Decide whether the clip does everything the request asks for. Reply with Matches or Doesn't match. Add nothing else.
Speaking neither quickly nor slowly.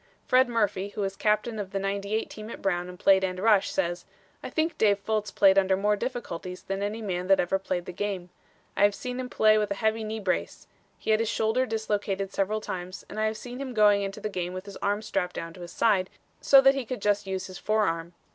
Doesn't match